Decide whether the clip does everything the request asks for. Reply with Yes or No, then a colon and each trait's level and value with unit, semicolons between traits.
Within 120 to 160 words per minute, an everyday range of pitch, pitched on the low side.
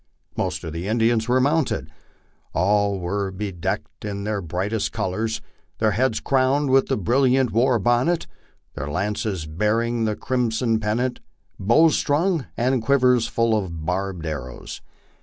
Yes: average, 140 wpm; average, 4.6 semitones; low, 110 Hz